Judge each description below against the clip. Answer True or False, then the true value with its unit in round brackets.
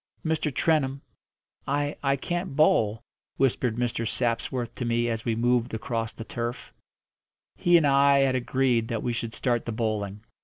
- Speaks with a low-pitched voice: True (120 Hz)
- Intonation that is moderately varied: True (3.1 semitones)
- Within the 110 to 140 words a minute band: False (160 wpm)